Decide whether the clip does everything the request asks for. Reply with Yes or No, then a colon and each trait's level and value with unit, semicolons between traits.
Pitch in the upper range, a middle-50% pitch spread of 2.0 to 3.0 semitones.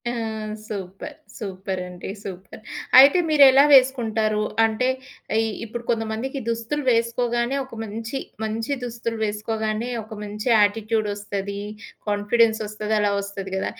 Yes: high, 220 Hz; narrow, 2.4 semitones